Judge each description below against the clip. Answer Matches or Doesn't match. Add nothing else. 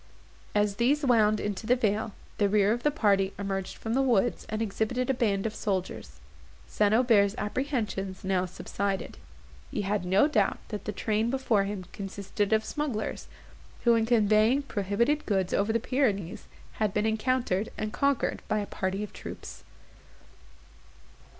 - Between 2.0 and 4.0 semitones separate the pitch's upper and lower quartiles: Matches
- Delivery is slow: Doesn't match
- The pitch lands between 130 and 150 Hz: Doesn't match